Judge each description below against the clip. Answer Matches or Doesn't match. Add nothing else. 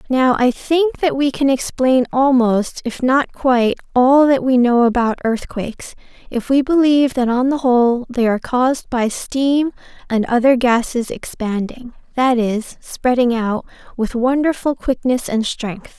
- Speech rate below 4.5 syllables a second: Matches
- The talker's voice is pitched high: Matches